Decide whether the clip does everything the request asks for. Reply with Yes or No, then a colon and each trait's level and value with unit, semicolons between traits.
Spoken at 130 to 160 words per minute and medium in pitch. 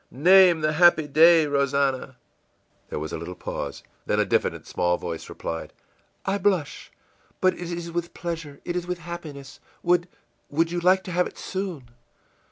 No: average, 175 wpm; medium, 170 Hz